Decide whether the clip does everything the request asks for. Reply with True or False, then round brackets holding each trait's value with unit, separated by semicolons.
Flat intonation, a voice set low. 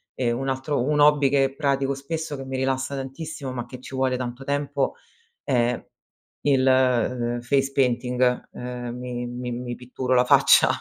True (1.8 semitones; 130 Hz)